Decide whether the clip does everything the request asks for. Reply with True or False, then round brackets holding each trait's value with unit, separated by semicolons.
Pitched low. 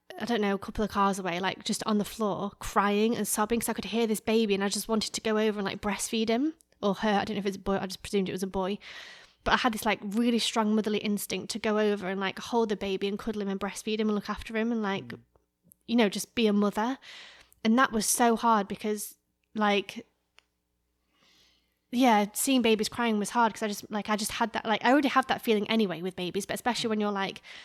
False (215 Hz)